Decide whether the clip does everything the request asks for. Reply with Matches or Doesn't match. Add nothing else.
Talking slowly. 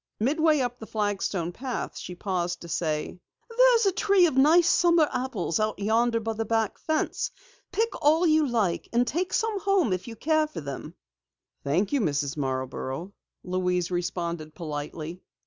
Doesn't match